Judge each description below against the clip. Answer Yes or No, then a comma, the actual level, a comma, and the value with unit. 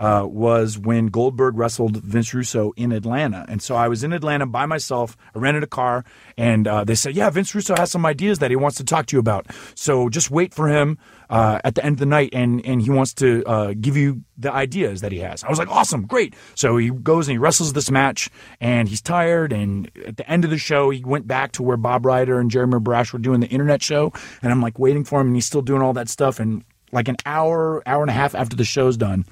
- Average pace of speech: No, fast, 260 wpm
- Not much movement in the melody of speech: No, average, 3.8 semitones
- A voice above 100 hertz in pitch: Yes, low, 130 Hz